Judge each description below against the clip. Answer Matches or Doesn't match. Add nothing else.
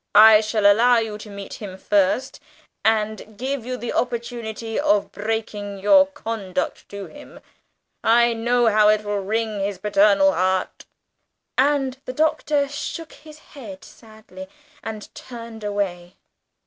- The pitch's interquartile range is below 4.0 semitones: Matches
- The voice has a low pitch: Doesn't match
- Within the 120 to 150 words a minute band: Matches